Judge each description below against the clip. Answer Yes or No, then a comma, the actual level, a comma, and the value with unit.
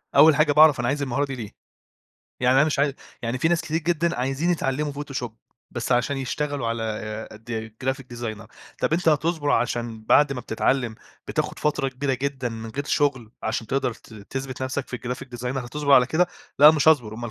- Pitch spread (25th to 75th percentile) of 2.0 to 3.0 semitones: No, average, 3.5 semitones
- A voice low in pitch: Yes, low, 130 Hz